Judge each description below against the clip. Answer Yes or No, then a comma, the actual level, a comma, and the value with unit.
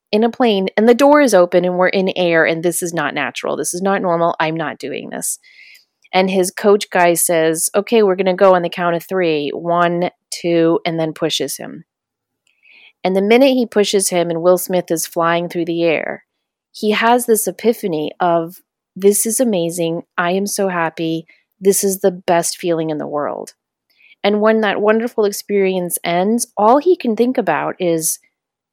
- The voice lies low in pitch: No, medium, 185 Hz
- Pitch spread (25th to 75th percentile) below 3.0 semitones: No, average, 3.5 semitones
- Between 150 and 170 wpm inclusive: No, average, 190 wpm